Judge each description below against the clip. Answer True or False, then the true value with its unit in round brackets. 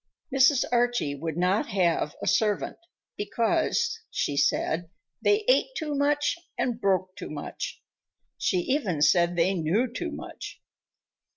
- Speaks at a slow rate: True (130 wpm)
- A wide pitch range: True (8.0 semitones)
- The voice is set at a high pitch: True (200 Hz)